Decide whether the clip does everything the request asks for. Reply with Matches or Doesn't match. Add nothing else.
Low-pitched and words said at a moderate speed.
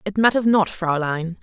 Doesn't match